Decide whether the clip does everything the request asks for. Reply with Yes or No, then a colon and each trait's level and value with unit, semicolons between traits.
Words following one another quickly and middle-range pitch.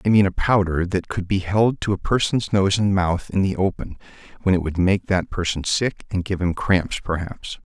No: fast, 225 wpm; very low, 95 Hz